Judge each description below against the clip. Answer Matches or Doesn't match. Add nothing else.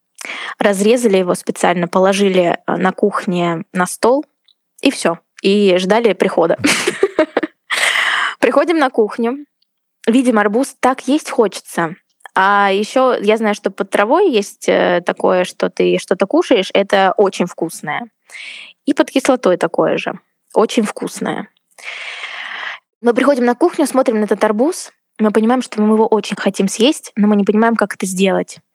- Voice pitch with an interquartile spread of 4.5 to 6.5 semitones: Matches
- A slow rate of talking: Doesn't match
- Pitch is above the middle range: Matches